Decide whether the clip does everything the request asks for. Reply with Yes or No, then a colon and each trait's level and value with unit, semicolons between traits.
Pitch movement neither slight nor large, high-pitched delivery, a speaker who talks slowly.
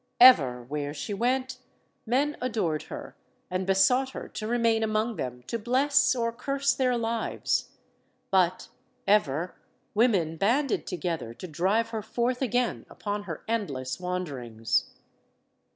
No: wide, 6.5 semitones; high, 215 Hz; slow, 130 wpm